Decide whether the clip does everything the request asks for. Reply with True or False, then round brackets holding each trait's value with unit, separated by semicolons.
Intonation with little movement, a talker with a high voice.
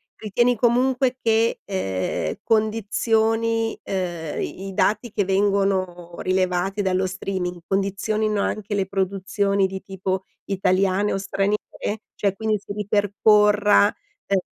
True (2.1 semitones; 200 Hz)